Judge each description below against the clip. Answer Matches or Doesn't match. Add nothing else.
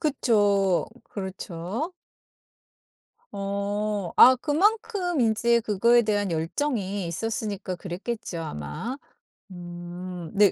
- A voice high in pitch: Matches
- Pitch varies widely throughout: Doesn't match